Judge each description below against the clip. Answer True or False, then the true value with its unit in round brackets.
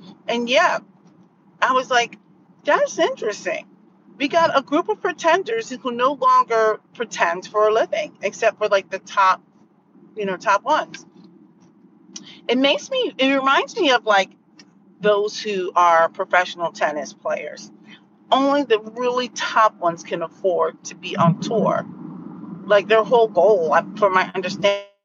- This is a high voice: True (215 Hz)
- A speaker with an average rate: True (150 wpm)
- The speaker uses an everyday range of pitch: False (6.0 semitones)